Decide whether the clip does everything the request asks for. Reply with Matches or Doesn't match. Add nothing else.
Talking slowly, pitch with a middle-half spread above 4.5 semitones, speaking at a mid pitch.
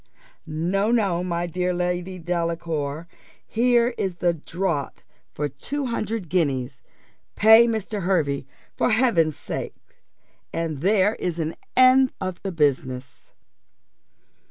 Matches